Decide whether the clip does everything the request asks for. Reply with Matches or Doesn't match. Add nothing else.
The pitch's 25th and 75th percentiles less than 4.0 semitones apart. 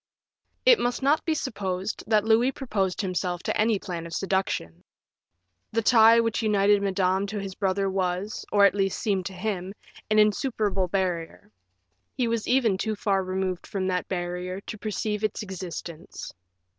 Matches